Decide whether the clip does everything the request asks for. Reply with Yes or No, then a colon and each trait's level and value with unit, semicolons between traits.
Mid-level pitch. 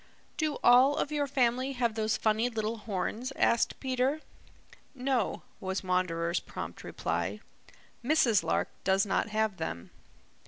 No: high, 225 Hz